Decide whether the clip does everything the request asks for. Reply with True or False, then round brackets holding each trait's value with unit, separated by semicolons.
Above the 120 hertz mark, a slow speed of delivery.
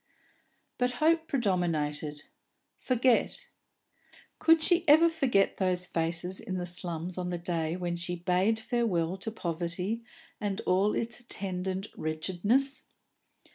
True (185 Hz; 120 wpm)